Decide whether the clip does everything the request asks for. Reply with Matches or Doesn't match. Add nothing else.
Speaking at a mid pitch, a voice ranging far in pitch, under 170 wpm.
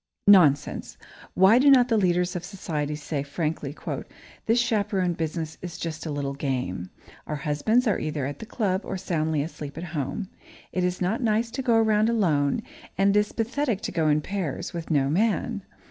Doesn't match